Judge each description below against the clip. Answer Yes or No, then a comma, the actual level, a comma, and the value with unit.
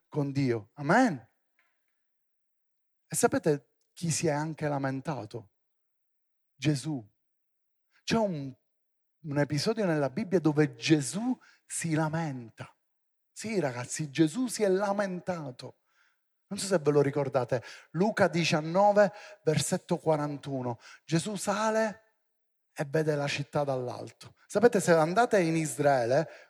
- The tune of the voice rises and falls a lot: Yes, wide, 5.8 semitones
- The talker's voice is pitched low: No, medium, 155 Hz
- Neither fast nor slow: No, slow, 110 wpm